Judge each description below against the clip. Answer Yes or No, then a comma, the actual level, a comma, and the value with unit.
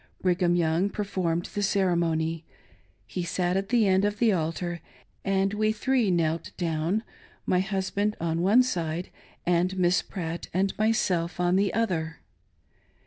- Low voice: No, medium, 180 Hz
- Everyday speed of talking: Yes, average, 150 wpm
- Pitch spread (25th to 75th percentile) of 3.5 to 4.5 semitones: No, average, 3.0 semitones